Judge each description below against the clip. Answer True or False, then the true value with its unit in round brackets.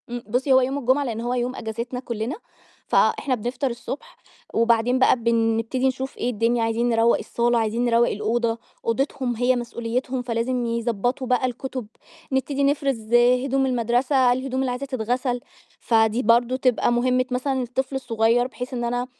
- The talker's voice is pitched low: False (245 Hz)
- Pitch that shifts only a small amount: True (1.9 semitones)